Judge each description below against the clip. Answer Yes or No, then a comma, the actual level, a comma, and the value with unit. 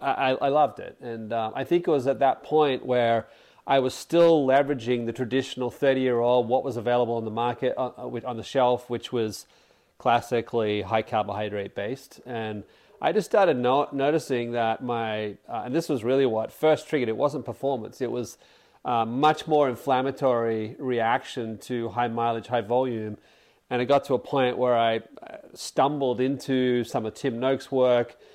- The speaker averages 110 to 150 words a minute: No, average, 180 wpm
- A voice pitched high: No, low, 125 Hz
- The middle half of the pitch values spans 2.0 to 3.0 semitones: Yes, narrow, 2.5 semitones